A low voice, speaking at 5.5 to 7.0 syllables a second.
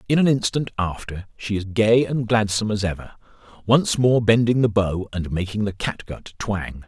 No: low, 105 Hz; 4.9 syllables/s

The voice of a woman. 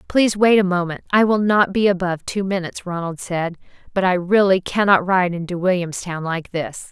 Yes: female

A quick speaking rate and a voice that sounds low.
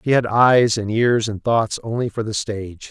Yes: fast, 225 wpm; low, 110 Hz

